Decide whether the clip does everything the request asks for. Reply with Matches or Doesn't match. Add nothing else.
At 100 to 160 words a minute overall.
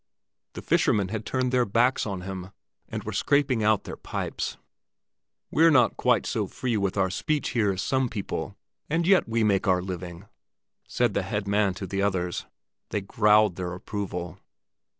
Doesn't match